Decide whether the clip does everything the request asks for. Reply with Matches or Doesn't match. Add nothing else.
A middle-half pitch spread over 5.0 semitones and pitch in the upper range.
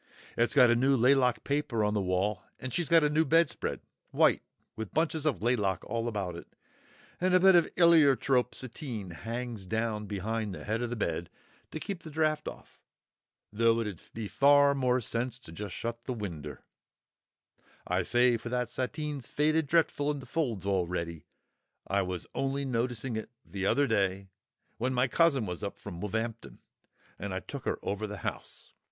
Doesn't match